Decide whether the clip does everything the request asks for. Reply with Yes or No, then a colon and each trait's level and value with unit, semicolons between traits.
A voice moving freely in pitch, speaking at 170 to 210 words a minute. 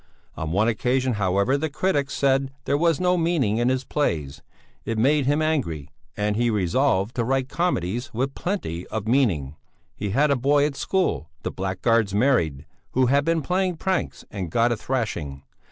Yes: wide, 6.2 semitones; average, 175 wpm